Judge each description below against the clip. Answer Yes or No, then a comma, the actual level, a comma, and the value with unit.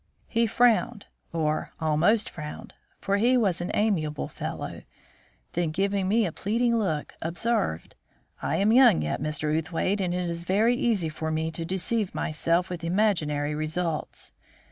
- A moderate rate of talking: Yes, average, 150 wpm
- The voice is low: No, medium, 175 Hz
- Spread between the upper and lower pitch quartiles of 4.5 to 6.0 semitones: Yes, average, 5.1 semitones